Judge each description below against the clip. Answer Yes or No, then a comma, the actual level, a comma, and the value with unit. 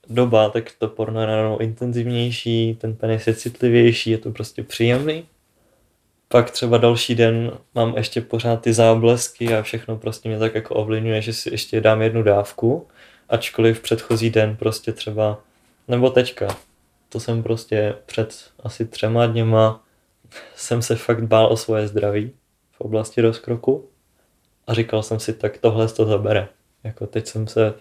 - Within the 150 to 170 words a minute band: Yes, average, 160 wpm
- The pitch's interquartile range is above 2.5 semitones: No, narrow, 1.2 semitones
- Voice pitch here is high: No, low, 115 Hz